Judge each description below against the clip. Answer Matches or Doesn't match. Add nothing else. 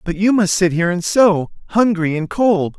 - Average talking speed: Doesn't match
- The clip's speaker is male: Matches